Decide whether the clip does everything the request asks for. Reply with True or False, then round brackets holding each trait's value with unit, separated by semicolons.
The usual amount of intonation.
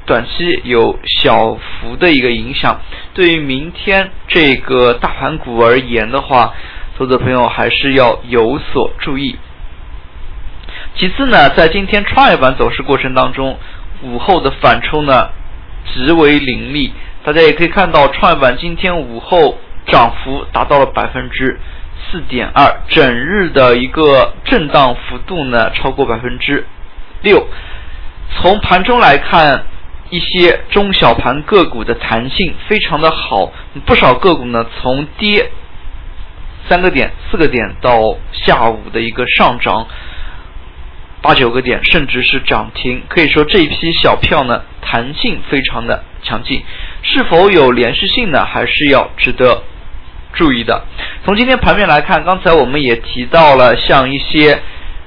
False (9.0 semitones)